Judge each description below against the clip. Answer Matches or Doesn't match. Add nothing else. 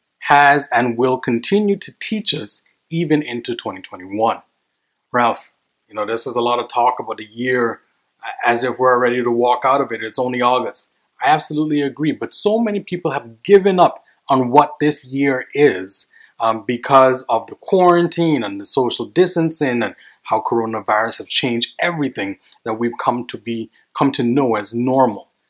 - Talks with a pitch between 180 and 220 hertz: Doesn't match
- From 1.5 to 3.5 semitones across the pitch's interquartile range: Doesn't match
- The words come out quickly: Doesn't match